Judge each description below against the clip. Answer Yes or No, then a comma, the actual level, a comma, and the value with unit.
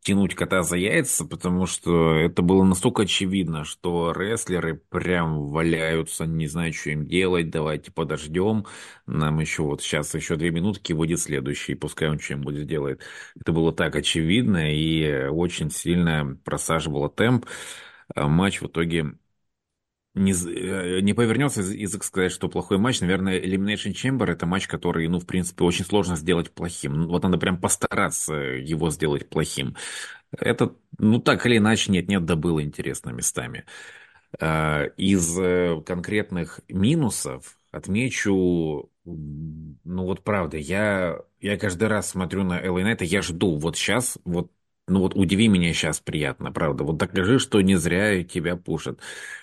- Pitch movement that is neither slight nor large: Yes, average, 3.0 semitones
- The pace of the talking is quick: No, average, 145 wpm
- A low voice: Yes, very low, 90 Hz